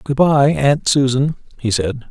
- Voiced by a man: Yes, male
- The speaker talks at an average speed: Yes, average, 170 wpm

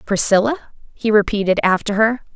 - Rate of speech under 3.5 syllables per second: No, 5.6 syllables/s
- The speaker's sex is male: No, female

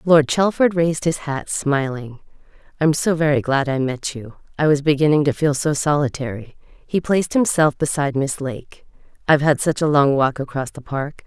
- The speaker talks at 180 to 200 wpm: Yes, average, 190 wpm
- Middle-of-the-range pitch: Yes, medium, 145 Hz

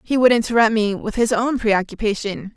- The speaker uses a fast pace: No, average, 190 wpm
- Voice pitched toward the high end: Yes, high, 225 Hz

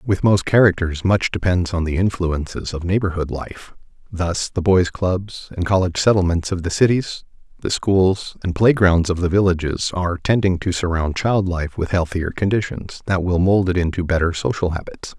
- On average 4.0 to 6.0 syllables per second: Yes, 5.0 syllables/s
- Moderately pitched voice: No, very low, 90 Hz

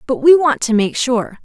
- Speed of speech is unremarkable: No, fast, 250 wpm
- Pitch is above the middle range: Yes, very high, 250 Hz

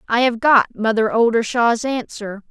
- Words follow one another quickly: No, average, 145 wpm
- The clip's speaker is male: No, female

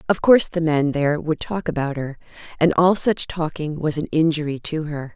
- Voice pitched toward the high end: No, medium, 155 Hz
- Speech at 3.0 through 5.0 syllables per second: No, 5.4 syllables/s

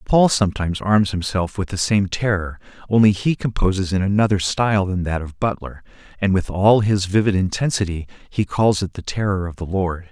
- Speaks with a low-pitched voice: Yes, very low, 95 Hz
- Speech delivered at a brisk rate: No, average, 190 wpm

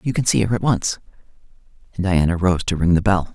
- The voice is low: Yes, very low, 95 Hz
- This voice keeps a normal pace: No, fast, 235 wpm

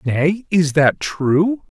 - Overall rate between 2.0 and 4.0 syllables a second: Yes, 2.7 syllables/s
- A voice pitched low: No, medium, 165 Hz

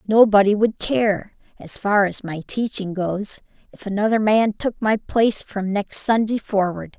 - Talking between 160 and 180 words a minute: Yes, average, 165 wpm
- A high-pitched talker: Yes, high, 205 Hz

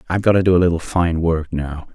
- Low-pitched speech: Yes, very low, 85 Hz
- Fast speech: Yes, fast, 275 wpm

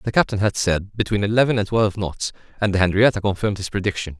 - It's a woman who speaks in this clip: No, male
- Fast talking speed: Yes, fast, 215 wpm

